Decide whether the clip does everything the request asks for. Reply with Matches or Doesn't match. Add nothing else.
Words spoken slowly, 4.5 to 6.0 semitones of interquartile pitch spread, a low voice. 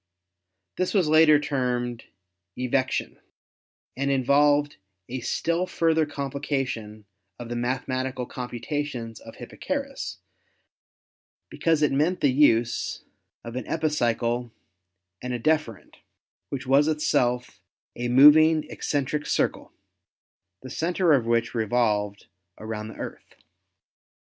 Doesn't match